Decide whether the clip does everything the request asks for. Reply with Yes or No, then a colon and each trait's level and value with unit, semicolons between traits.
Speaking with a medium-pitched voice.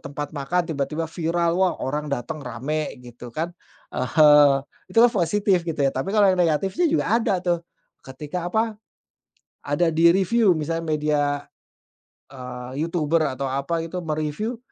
Yes: medium, 160 Hz